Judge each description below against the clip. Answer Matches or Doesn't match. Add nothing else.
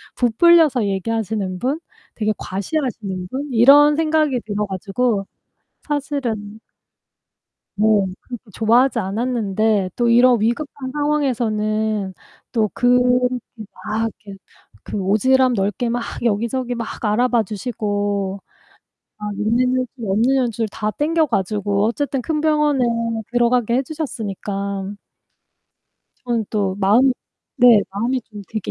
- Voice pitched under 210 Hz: Doesn't match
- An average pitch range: Matches